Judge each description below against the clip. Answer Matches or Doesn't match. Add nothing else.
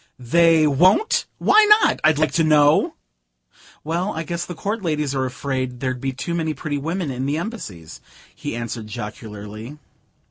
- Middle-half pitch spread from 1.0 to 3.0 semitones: Doesn't match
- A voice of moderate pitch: Matches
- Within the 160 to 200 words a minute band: Matches